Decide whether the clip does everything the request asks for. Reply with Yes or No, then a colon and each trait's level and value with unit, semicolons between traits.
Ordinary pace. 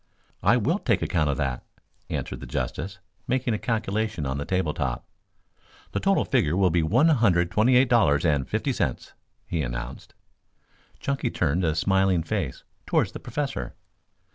Yes: average, 165 wpm